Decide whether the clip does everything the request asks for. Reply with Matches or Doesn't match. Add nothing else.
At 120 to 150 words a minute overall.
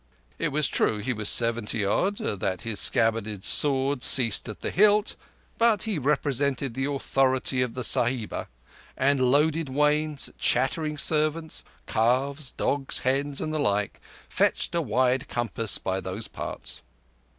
Matches